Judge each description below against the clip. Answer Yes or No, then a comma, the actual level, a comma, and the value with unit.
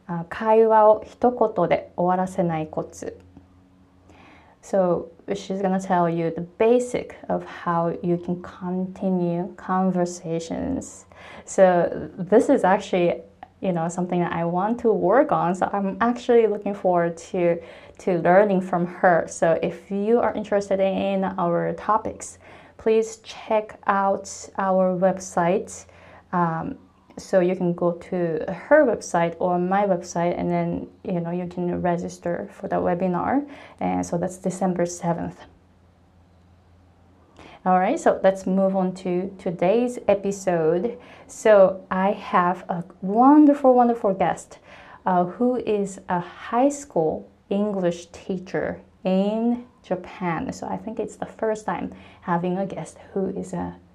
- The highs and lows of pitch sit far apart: No, average, 2.8 semitones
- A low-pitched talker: No, medium, 185 Hz